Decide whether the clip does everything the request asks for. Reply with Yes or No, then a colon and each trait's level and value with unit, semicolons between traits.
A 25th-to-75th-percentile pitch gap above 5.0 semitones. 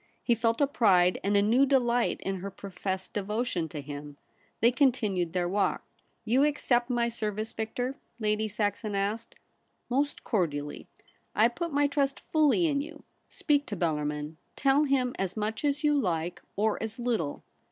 Yes: wide, 5.6 semitones